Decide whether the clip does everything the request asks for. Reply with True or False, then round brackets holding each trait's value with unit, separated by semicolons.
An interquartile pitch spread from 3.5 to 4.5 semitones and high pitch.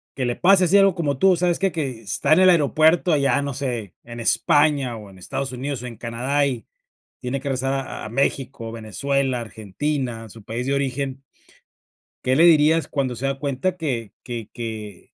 False (4.0 semitones; 135 Hz)